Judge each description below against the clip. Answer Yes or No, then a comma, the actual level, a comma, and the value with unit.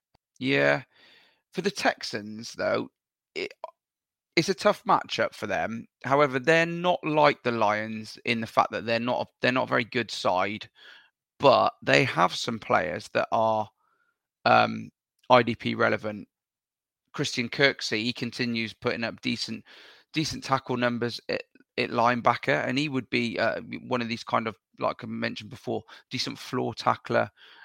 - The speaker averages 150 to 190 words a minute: Yes, average, 155 wpm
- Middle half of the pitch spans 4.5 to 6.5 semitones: Yes, average, 5.1 semitones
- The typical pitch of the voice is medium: No, low, 120 Hz